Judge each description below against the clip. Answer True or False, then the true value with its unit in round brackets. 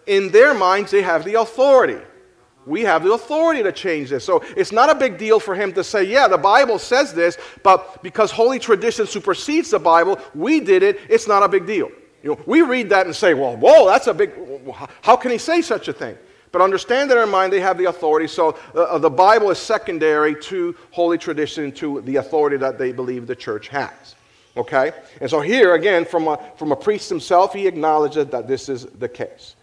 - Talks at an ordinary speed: False (220 wpm)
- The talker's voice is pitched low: False (195 Hz)